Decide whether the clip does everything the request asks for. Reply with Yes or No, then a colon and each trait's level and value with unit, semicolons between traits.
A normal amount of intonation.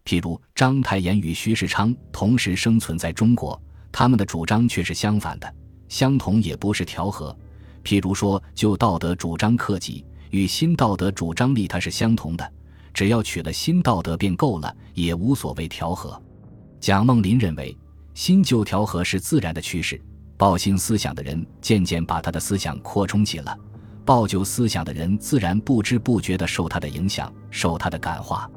Yes: average, 4.7 semitones